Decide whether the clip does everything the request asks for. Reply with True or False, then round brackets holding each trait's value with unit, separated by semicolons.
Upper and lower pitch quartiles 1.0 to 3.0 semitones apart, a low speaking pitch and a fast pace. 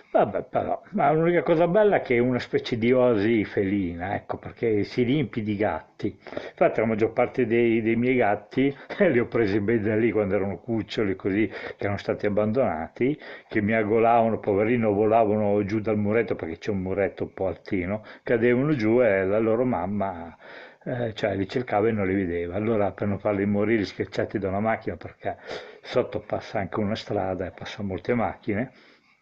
True (2.7 semitones; 110 Hz; 185 wpm)